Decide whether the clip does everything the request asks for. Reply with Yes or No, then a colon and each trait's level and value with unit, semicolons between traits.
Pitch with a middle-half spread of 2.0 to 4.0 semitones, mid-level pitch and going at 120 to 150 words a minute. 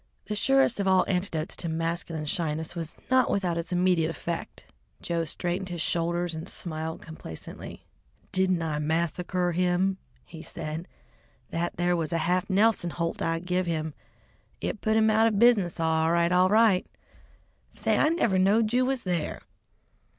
No: average, 2.7 semitones; medium, 175 Hz; average, 160 wpm